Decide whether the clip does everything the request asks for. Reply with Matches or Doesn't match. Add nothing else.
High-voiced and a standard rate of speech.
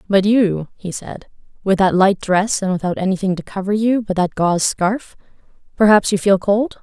Matches